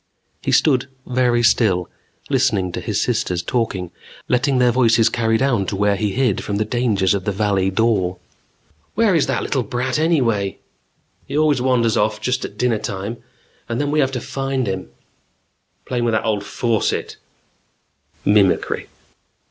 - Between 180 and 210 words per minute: No, average, 165 wpm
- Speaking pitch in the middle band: No, low, 115 Hz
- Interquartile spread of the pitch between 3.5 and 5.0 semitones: Yes, average, 4.1 semitones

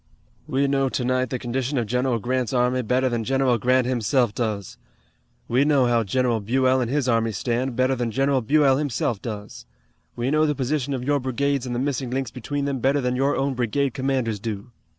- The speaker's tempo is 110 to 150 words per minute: No, average, 200 wpm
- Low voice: Yes, low, 130 Hz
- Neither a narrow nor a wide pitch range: No, narrow, 2.2 semitones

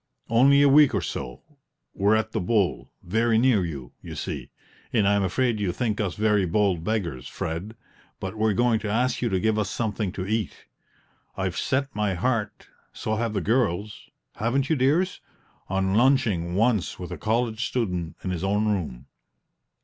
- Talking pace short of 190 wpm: Yes, average, 175 wpm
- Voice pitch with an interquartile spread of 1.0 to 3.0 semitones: No, average, 3.7 semitones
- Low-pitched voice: Yes, low, 105 Hz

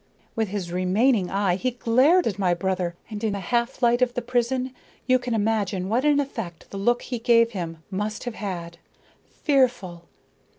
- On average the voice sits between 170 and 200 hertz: No, high, 220 Hz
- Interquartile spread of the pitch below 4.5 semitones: No, average, 4.8 semitones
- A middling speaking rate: Yes, average, 180 wpm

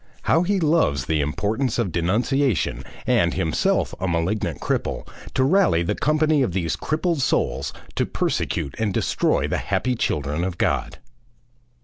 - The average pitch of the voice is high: No, low, 105 Hz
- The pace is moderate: Yes, average, 145 wpm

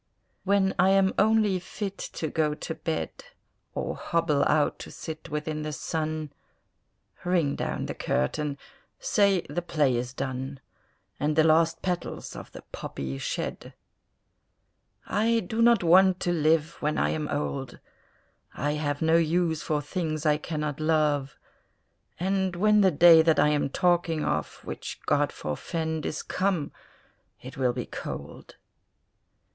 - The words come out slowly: No, average, 145 wpm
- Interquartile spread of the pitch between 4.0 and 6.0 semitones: No, average, 3.2 semitones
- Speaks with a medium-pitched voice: Yes, medium, 160 Hz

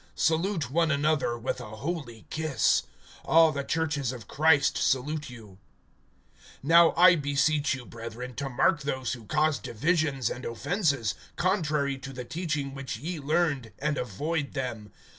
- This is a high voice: No, medium, 140 Hz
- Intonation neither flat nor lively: Yes, average, 4.1 semitones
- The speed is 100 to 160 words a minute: Yes, average, 145 wpm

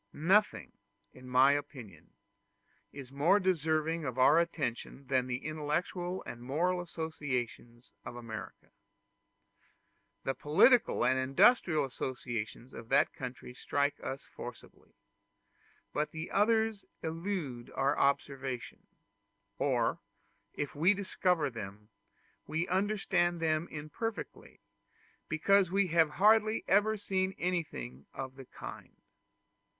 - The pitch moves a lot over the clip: Yes, wide, 5.8 semitones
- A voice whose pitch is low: No, medium, 150 Hz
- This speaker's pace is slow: Yes, slow, 110 wpm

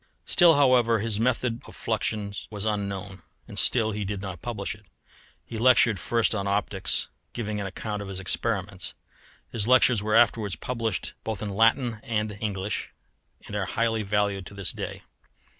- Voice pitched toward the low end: Yes, low, 105 Hz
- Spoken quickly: No, average, 165 wpm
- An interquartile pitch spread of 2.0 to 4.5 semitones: Yes, narrow, 2.5 semitones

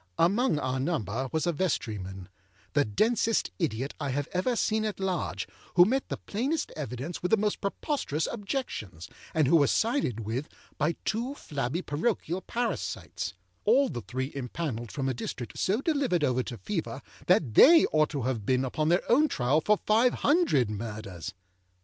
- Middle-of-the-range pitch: Yes, medium, 155 Hz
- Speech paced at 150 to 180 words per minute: Yes, average, 160 wpm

